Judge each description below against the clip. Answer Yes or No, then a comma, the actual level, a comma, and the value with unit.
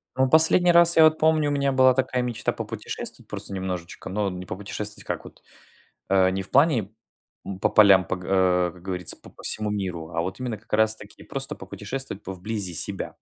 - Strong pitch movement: Yes, wide, 5.9 semitones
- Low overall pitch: Yes, low, 105 Hz